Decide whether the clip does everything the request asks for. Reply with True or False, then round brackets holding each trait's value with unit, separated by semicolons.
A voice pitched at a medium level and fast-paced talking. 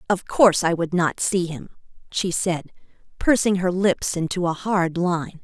False (180 Hz; 175 wpm)